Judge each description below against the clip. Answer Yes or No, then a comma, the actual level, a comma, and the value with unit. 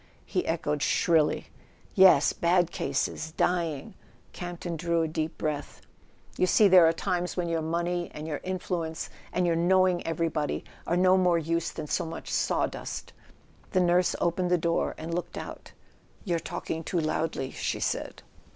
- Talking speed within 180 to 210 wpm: No, average, 160 wpm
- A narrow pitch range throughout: Yes, narrow, 1.9 semitones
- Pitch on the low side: No, medium, 170 Hz